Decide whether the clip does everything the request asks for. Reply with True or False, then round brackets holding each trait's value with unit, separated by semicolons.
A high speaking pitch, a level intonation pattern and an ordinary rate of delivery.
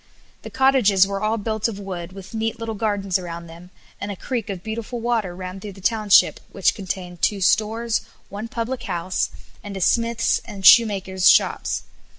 False (205 Hz; 3.2 semitones; 170 wpm)